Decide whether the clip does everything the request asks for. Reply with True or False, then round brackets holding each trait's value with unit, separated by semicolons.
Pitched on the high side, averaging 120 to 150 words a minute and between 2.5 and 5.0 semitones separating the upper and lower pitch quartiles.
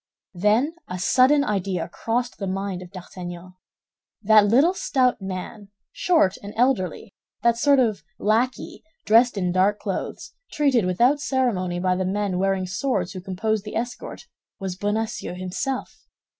True (205 Hz; 145 wpm; 4.7 semitones)